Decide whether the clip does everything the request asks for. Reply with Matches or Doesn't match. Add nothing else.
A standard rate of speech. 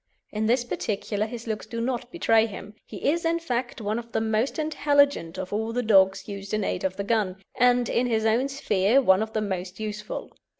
Doesn't match